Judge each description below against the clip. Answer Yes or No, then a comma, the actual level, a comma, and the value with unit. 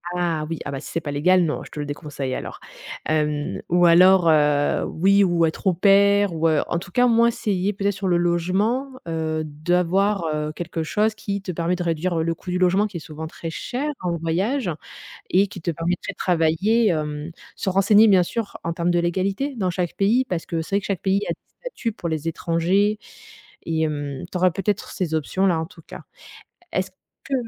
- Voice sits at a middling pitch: Yes, medium, 175 Hz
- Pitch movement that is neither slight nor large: Yes, average, 3.5 semitones